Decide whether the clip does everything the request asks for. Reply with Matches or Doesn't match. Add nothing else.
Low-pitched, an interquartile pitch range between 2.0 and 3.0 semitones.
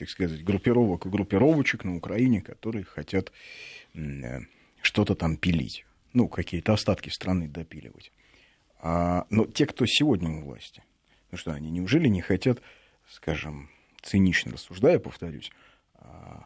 Doesn't match